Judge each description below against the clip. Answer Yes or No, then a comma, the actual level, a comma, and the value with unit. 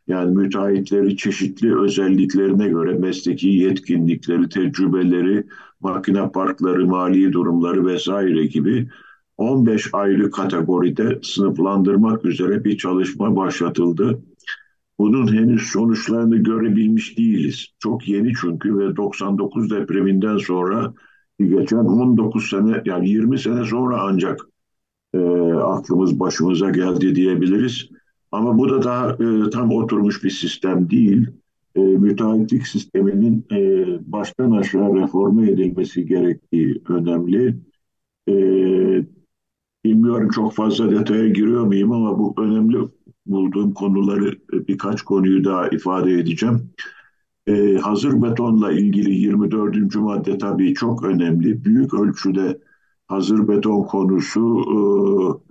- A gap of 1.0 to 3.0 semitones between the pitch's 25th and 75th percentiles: Yes, average, 2.7 semitones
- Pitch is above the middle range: No, low, 100 Hz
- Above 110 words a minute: No, average, 105 wpm